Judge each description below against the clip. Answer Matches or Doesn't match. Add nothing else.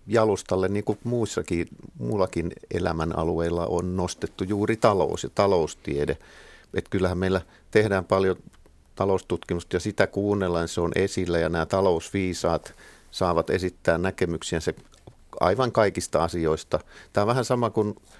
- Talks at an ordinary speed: Matches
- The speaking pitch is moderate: Doesn't match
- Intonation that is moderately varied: Matches